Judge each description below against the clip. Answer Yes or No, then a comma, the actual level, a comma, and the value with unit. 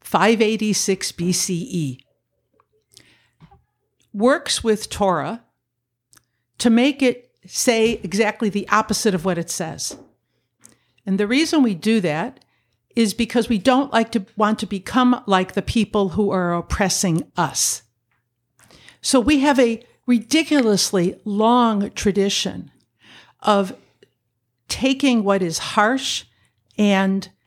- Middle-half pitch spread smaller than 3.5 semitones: No, average, 4.2 semitones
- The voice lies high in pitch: Yes, high, 210 Hz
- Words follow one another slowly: Yes, slow, 110 wpm